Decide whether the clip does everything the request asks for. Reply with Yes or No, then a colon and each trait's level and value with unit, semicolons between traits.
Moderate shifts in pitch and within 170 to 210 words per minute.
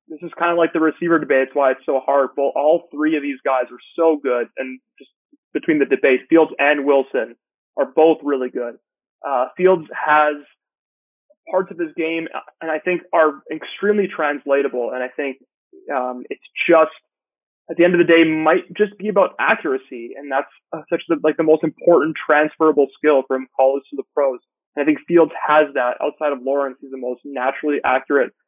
Yes: average, 3.5 semitones; average, 200 wpm